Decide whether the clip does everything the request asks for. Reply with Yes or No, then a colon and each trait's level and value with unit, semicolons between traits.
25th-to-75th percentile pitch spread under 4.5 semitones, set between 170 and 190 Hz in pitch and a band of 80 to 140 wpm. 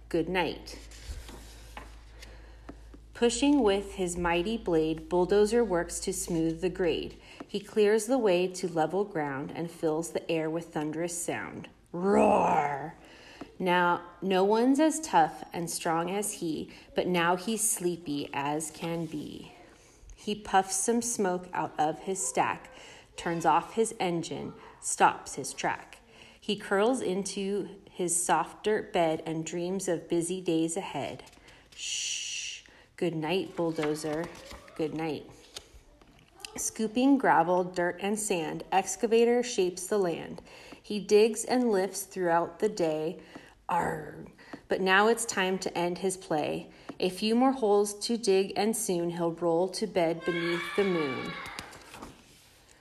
Yes: average, 3.6 semitones; medium, 185 Hz; slow, 135 wpm